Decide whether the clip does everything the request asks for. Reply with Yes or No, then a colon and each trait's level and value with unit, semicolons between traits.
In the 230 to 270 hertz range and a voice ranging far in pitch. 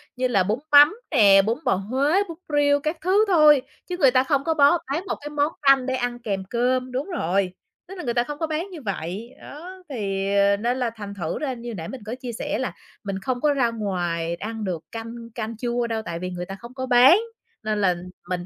Yes: high, 240 Hz; wide, 6.2 semitones